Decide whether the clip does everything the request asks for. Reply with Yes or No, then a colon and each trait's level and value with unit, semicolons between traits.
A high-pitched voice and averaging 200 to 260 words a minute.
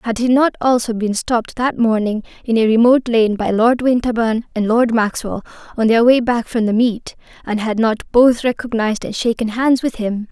Yes: high, 230 Hz; fast, 205 wpm